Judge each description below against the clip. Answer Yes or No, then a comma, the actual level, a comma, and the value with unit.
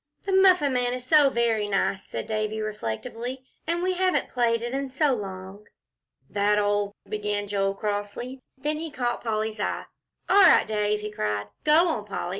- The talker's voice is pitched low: No, high, 220 Hz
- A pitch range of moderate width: Yes, average, 4.6 semitones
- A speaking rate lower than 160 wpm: No, average, 180 wpm